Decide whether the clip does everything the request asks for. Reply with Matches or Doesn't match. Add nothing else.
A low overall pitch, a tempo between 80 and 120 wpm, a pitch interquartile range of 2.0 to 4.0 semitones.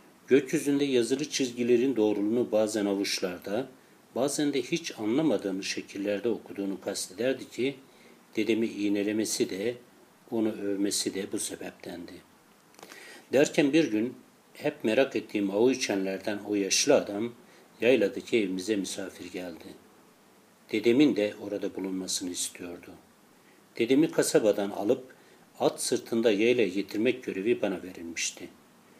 Matches